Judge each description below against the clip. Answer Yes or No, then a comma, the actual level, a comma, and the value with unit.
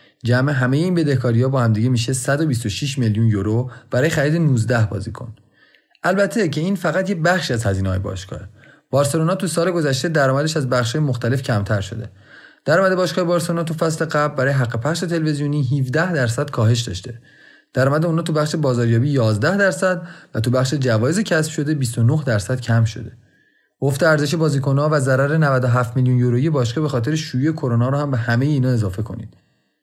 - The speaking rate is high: Yes, fast, 175 wpm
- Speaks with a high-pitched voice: No, low, 135 Hz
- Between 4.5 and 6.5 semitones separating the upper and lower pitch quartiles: Yes, average, 4.8 semitones